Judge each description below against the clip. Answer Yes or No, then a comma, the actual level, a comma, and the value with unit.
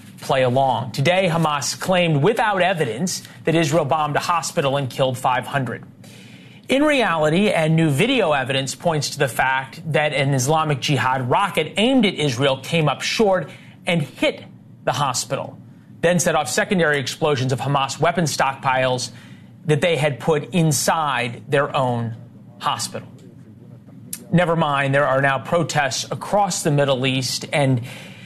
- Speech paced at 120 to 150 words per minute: Yes, average, 145 wpm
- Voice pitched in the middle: Yes, medium, 150 Hz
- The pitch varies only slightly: No, average, 3.9 semitones